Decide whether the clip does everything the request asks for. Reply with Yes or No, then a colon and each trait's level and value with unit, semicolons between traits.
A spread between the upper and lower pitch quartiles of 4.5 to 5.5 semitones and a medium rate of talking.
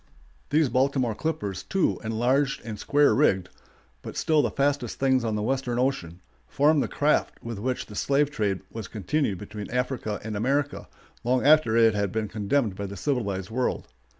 Yes: average, 5.0 semitones; average, 180 wpm